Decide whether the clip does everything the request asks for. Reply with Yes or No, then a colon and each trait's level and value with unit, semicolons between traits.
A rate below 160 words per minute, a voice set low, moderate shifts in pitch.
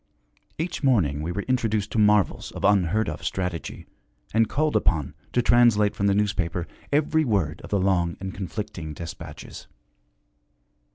Yes: average, 150 wpm; low, 100 Hz; average, 4.3 semitones